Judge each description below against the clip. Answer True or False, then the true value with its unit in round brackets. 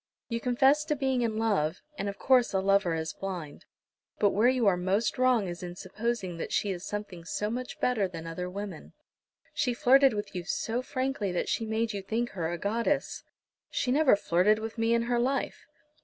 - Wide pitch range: False (4.6 semitones)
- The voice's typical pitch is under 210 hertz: False (215 Hz)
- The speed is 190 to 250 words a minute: True (200 wpm)